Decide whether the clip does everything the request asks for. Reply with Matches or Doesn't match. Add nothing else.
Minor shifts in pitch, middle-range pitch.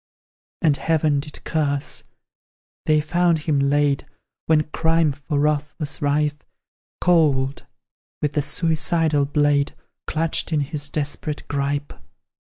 Matches